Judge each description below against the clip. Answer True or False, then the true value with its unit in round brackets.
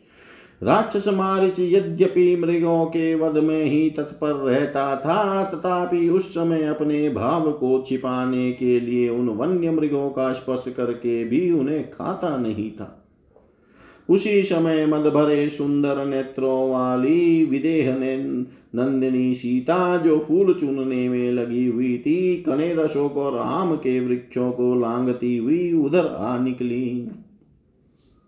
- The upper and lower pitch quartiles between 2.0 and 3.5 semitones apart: False (5.2 semitones)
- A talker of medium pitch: True (145 Hz)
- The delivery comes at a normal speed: True (125 wpm)